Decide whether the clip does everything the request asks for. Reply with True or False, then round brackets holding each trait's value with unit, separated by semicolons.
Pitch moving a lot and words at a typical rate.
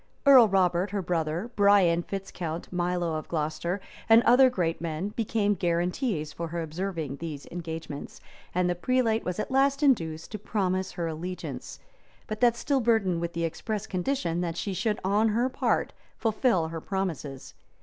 False (4.5 semitones; 165 wpm)